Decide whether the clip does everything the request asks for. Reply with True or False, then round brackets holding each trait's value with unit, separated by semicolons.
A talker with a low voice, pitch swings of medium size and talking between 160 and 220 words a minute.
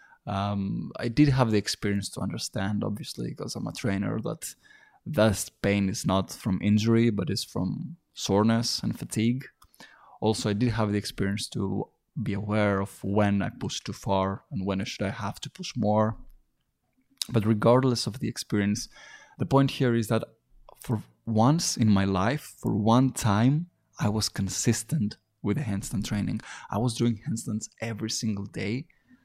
True (110 Hz; 3.6 semitones; 170 wpm)